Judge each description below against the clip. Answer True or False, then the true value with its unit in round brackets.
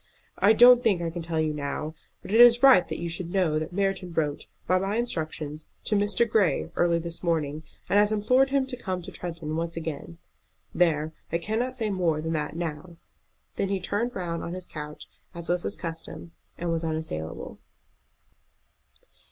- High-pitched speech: False (170 Hz)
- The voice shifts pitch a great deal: False (4.1 semitones)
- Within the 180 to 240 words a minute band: True (185 wpm)